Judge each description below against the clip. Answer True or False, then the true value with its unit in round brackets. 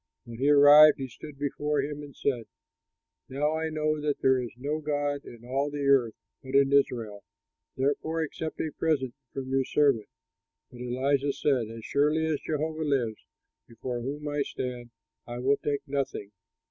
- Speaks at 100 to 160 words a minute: False (170 wpm)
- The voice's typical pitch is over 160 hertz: False (140 Hz)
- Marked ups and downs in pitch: False (2.7 semitones)